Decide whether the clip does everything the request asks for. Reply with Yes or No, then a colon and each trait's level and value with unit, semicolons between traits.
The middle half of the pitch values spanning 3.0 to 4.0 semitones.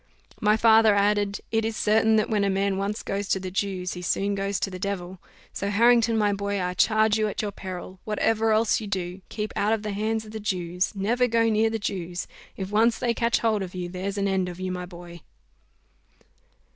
No: narrow, 2.6 semitones